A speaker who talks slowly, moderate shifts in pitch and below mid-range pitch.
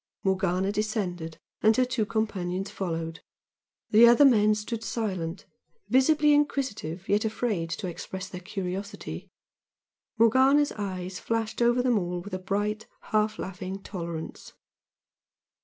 No: slow, 125 wpm; average, 3.8 semitones; high, 205 Hz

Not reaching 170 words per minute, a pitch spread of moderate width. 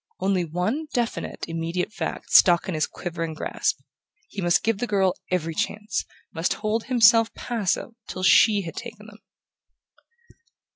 Yes: average, 145 wpm; average, 4.5 semitones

